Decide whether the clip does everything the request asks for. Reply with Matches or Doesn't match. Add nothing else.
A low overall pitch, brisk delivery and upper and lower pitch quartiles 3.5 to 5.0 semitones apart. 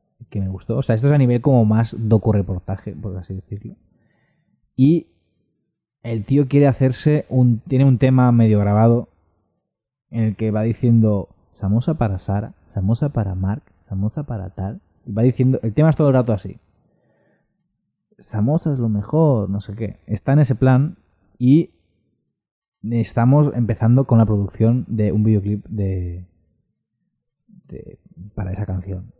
Doesn't match